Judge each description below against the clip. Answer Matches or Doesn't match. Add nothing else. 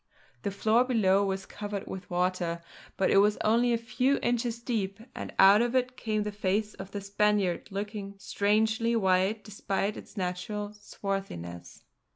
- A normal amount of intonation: Doesn't match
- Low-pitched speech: Doesn't match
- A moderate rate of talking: Matches